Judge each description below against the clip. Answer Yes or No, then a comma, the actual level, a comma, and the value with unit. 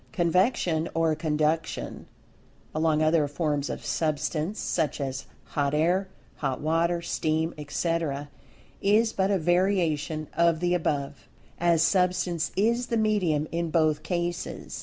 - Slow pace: Yes, slow, 125 wpm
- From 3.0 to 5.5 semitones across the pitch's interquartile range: No, narrow, 2.6 semitones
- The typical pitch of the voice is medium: Yes, medium, 165 Hz